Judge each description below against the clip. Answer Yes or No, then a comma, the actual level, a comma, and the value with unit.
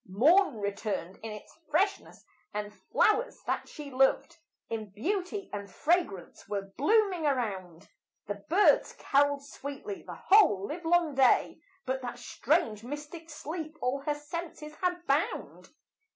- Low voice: No, very high, 285 Hz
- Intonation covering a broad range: Yes, wide, 8.0 semitones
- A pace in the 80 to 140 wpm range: Yes, slow, 135 wpm